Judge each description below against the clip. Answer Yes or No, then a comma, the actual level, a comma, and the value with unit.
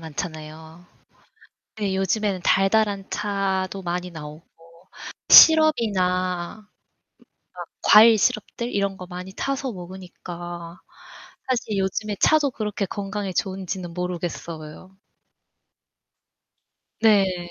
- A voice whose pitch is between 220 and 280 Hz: No, high, 190 Hz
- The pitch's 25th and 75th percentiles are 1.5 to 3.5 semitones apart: Yes, average, 3.0 semitones